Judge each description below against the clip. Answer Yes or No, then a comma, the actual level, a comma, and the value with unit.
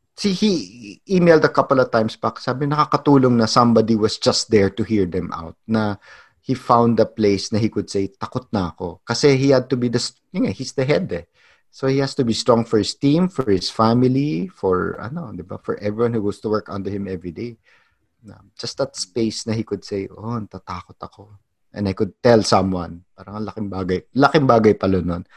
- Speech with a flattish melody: No, average, 4.4 semitones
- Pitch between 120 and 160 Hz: No, low, 110 Hz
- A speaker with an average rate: No, fast, 215 wpm